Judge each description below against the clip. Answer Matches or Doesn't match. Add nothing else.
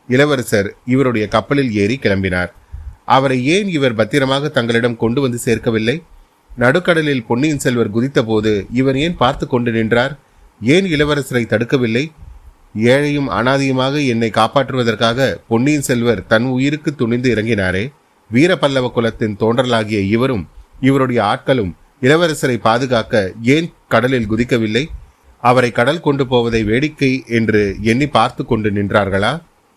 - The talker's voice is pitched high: Doesn't match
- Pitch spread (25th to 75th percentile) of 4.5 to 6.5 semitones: Doesn't match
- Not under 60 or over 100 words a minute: Doesn't match